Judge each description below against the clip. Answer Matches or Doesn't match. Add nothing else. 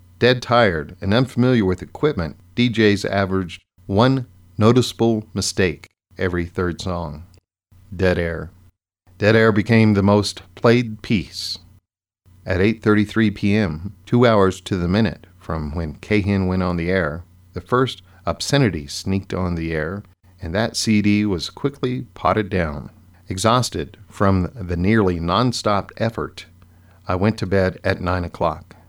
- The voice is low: Matches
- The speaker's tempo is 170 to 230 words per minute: Doesn't match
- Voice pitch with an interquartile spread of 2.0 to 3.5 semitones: Matches